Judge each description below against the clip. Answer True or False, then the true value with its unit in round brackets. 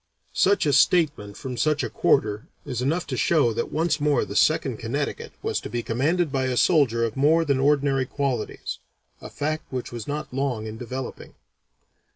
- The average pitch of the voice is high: False (135 Hz)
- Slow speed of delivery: False (185 wpm)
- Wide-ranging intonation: False (3.9 semitones)